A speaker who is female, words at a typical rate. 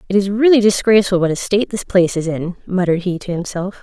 No: female; fast, 235 wpm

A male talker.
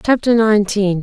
No: female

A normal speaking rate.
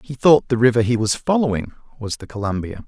No: fast, 210 wpm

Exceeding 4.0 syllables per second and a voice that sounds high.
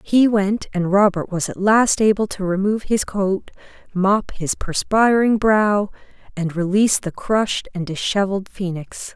Yes: 4.5 syllables/s; high, 200 Hz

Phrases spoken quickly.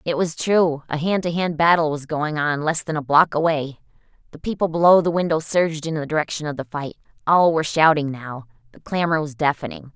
Yes: fast, 215 wpm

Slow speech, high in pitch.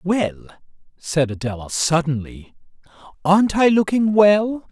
No: slow, 100 wpm; medium, 170 Hz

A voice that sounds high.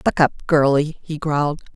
No: medium, 150 Hz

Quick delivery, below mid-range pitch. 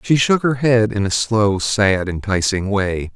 No: average, 190 wpm; low, 105 Hz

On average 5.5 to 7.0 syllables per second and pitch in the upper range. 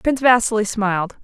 Yes: 5.9 syllables/s; high, 220 Hz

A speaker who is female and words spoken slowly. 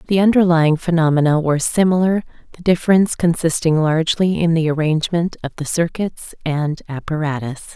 Yes: female; slow, 130 wpm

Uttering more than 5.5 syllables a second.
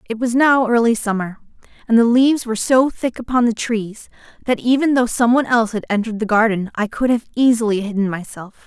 Yes: 6.0 syllables/s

